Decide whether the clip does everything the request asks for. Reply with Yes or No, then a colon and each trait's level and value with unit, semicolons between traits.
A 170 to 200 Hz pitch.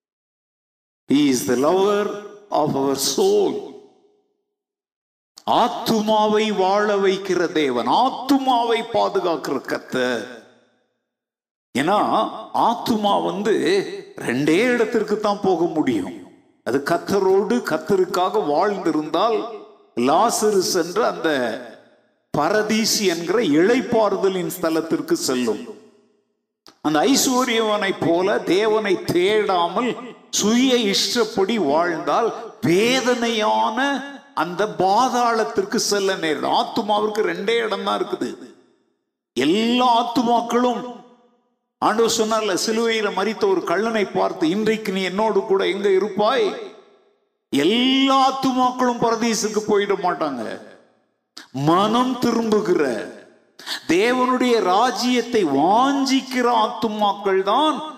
No: high, 230 Hz